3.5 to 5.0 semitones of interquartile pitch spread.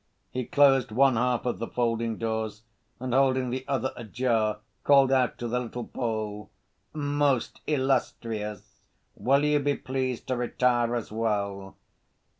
No: average, 3.0 semitones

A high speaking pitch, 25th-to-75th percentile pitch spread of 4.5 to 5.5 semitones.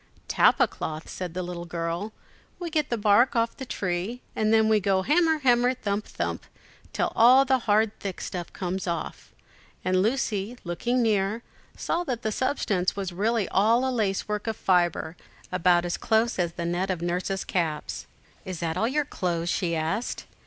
Yes: high, 200 Hz; average, 4.9 semitones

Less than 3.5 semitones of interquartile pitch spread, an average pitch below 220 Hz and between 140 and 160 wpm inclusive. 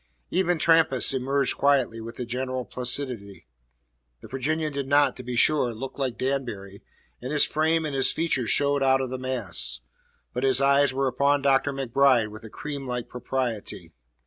No: narrow, 2.4 semitones; low, 135 Hz; average, 170 wpm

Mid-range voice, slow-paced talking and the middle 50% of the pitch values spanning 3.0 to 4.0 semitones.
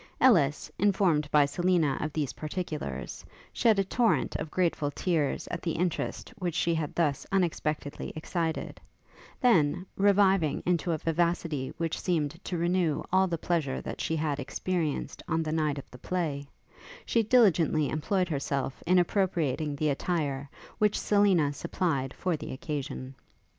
No: medium, 165 Hz; average, 150 wpm; average, 3.7 semitones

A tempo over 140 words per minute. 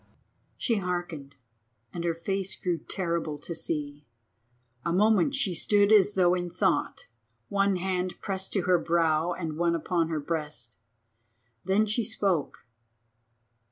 No: slow, 135 wpm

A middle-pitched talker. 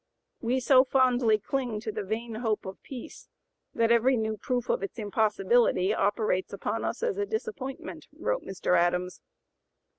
No: high, 230 Hz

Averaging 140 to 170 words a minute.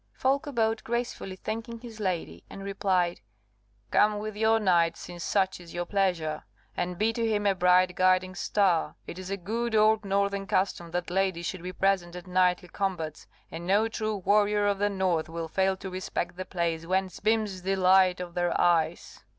No: average, 185 wpm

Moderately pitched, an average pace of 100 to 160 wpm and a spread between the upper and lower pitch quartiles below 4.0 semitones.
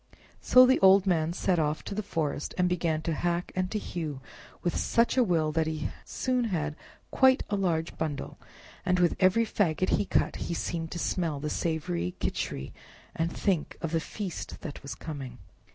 No: medium, 170 Hz; average, 185 wpm; average, 3.3 semitones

